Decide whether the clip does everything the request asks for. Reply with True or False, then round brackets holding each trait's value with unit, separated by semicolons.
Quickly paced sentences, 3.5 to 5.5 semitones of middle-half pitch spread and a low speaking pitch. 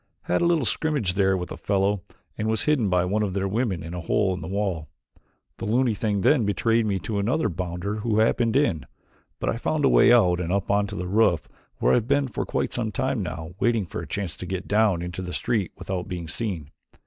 True (235 wpm; 3.9 semitones; 100 Hz)